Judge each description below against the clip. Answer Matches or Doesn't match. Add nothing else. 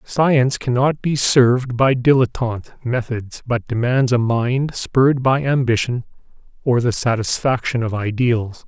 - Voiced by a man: Matches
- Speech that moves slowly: Matches